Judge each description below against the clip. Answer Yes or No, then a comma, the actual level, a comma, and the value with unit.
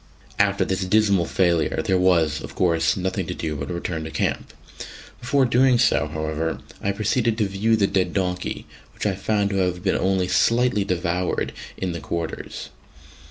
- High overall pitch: No, very low, 95 Hz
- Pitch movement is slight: No, average, 3.4 semitones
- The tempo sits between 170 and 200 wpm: Yes, average, 175 wpm